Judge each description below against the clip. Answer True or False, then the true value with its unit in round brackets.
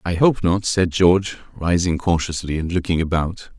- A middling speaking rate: True (165 wpm)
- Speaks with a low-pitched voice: True (90 Hz)